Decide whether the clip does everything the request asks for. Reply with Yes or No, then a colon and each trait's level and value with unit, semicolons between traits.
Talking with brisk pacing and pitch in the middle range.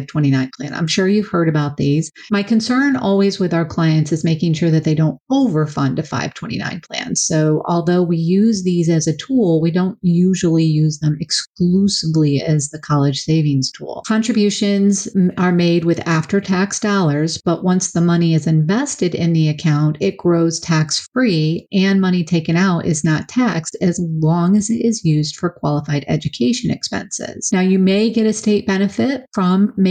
No: average, 175 wpm; medium, 170 Hz